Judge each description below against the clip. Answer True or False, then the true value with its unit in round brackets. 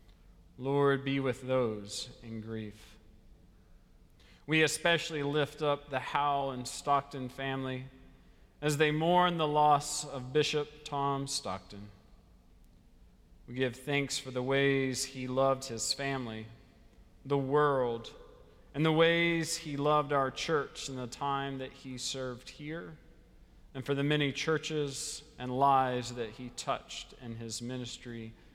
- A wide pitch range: False (3.4 semitones)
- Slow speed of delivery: True (130 wpm)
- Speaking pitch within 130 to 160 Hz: True (135 Hz)